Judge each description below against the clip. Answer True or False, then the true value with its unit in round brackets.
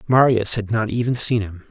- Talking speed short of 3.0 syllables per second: False (5.2 syllables/s)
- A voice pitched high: False (110 Hz)